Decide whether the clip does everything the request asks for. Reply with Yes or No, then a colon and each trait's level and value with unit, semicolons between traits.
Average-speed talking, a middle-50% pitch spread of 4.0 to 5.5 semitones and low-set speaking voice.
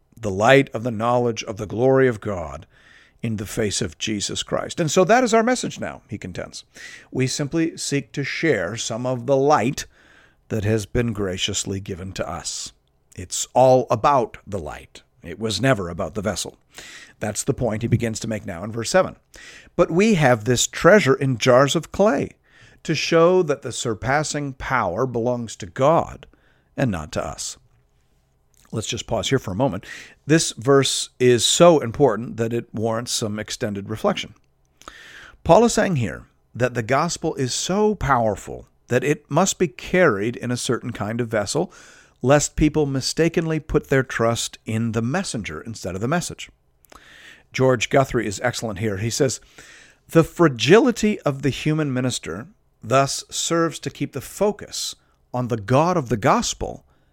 Yes: average, 170 wpm; average, 4.9 semitones; low, 125 Hz